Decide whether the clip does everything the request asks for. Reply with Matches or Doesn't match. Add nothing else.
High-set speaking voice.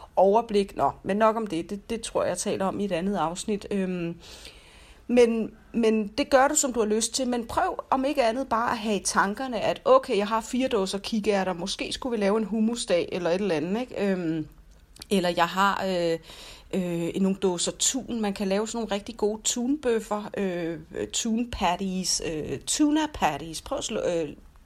Matches